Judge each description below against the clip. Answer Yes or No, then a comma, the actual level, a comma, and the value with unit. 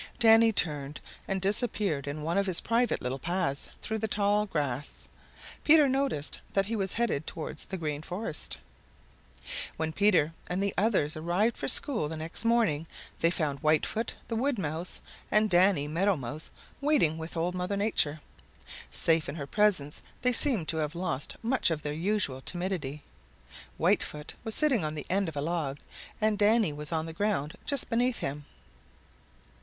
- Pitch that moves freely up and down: Yes, wide, 5.9 semitones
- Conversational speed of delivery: Yes, average, 170 wpm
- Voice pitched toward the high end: No, medium, 175 Hz